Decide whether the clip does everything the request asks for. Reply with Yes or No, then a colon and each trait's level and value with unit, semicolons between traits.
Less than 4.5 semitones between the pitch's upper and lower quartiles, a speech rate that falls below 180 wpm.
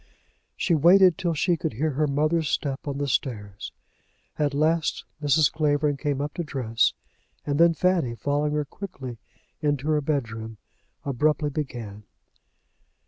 Yes: average, 2.8 semitones; average, 140 wpm